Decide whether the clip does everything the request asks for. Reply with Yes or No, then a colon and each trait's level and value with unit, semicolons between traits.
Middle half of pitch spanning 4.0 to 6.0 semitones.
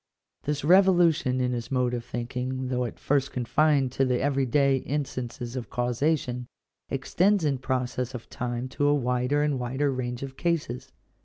No: narrow, 2.6 semitones